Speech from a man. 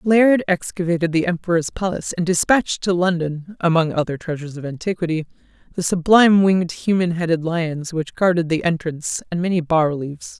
No: female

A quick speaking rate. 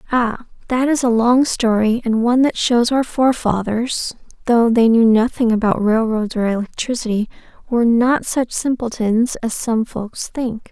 No: average, 155 wpm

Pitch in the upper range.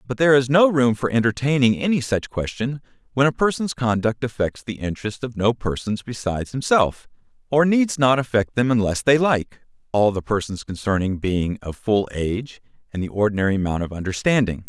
No: low, 115 Hz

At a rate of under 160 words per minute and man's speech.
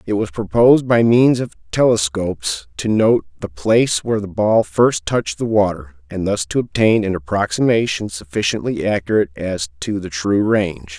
No: average, 170 wpm; male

